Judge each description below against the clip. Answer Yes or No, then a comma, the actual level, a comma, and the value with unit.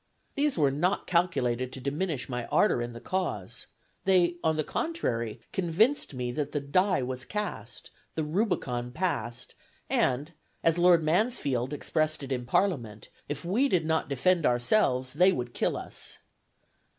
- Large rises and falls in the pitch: Yes, wide, 6.4 semitones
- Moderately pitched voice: Yes, medium, 155 Hz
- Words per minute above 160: No, average, 150 wpm